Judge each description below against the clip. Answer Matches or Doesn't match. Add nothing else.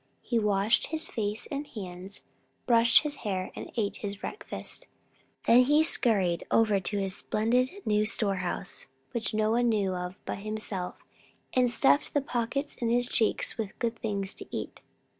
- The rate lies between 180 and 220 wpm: Doesn't match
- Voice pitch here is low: Doesn't match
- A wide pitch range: Doesn't match